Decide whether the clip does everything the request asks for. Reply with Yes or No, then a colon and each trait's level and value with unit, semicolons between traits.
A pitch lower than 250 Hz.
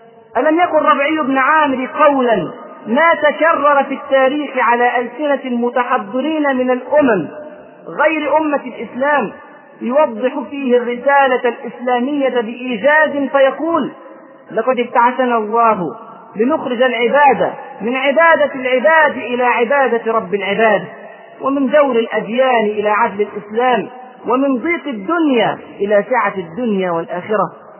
No: very high, 255 Hz